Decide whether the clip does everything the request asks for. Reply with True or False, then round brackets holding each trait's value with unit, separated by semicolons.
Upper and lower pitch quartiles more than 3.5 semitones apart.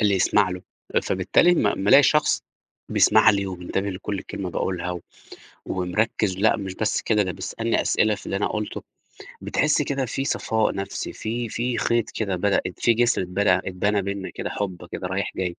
False (3.0 semitones)